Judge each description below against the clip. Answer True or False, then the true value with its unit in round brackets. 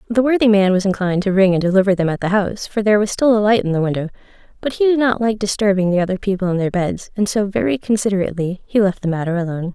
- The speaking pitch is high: True (200 Hz)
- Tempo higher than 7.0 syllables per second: True (7.2 syllables/s)